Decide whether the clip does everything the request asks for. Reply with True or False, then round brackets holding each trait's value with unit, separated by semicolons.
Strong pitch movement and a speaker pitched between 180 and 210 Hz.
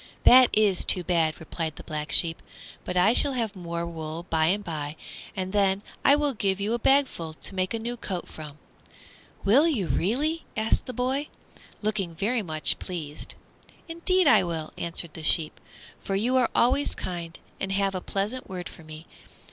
True (6.1 semitones; 190 Hz)